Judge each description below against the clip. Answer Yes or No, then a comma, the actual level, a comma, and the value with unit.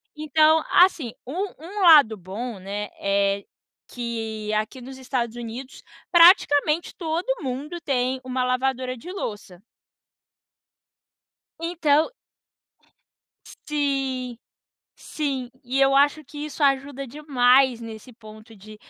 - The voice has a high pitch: Yes, very high, 260 Hz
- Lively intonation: No, average, 4.5 semitones